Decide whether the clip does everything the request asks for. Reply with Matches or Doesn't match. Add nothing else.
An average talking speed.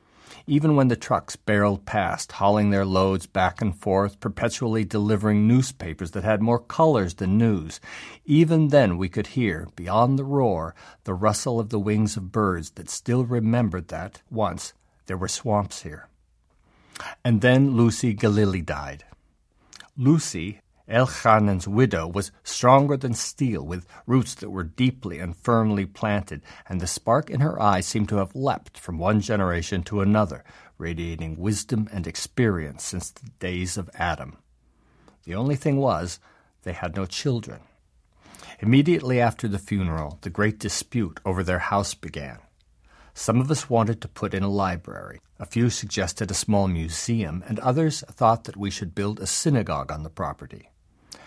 Matches